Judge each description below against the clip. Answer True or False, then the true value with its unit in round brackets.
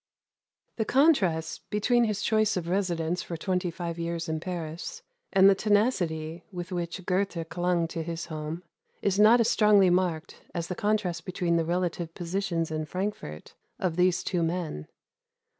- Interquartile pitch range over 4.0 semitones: False (3.0 semitones)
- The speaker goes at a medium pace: True (160 wpm)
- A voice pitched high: False (180 Hz)